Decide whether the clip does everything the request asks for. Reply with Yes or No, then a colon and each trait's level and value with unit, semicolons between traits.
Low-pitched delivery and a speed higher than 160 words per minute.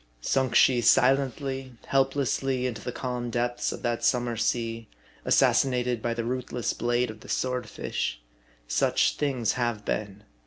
No: low, 120 Hz; average, 145 wpm